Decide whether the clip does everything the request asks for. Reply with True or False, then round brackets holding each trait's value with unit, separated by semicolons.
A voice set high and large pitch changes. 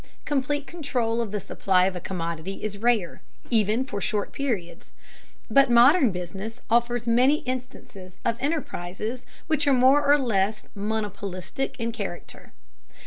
False (230 Hz; 4.9 semitones)